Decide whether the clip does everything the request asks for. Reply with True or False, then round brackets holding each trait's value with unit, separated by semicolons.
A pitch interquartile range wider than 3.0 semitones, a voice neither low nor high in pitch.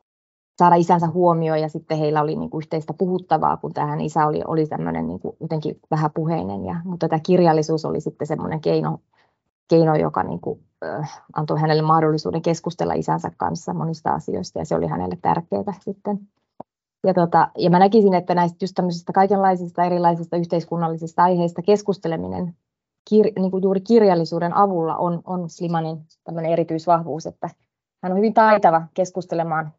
False (2.5 semitones; 170 Hz)